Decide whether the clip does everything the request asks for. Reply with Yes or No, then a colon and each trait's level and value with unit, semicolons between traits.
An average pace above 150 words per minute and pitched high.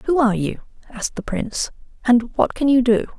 Yes: fast, 205 wpm; high, 235 Hz